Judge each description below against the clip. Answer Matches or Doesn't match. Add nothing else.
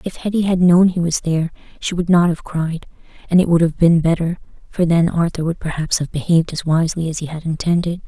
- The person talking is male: Doesn't match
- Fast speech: Matches